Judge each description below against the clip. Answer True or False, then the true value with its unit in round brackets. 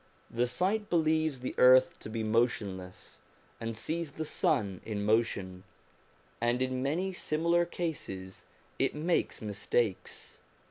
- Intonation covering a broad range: True (6.8 semitones)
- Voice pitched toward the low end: True (125 Hz)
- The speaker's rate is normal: False (125 wpm)